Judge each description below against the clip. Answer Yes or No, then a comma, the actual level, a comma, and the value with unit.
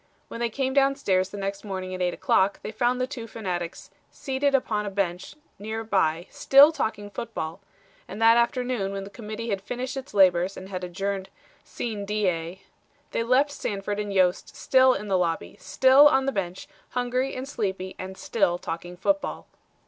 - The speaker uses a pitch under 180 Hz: No, high, 205 Hz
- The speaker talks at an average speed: Yes, average, 180 wpm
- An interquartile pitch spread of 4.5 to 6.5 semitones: Yes, average, 4.8 semitones